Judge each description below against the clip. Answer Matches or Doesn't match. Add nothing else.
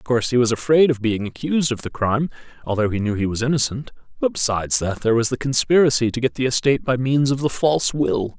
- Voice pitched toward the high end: Doesn't match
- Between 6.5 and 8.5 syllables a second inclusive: Matches